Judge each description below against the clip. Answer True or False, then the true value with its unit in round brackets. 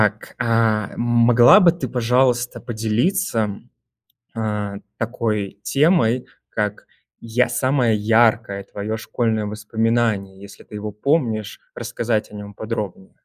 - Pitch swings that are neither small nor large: False (2.3 semitones)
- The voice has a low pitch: True (110 Hz)